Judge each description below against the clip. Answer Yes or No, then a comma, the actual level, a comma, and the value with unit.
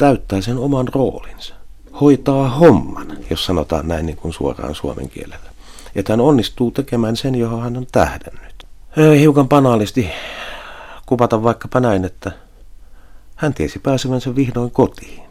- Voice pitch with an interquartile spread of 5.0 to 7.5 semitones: Yes, wide, 5.6 semitones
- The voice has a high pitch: No, low, 120 Hz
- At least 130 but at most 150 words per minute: Yes, average, 135 wpm